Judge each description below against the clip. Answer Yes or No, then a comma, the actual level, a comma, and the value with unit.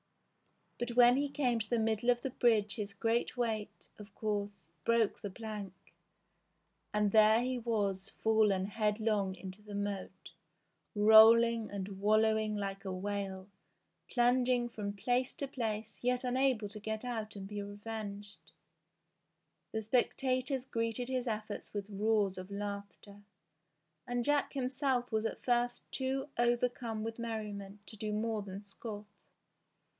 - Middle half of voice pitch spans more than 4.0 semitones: No, average, 2.9 semitones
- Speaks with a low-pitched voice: No, high, 220 Hz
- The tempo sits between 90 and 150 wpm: Yes, average, 140 wpm